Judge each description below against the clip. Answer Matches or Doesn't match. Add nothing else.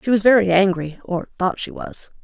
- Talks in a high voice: Matches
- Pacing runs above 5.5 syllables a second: Doesn't match